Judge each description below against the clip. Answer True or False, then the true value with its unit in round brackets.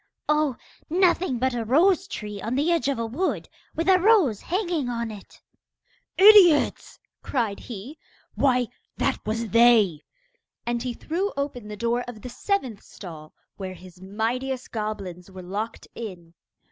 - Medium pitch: False (240 Hz)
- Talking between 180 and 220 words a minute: False (150 wpm)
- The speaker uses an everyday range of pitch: False (6.3 semitones)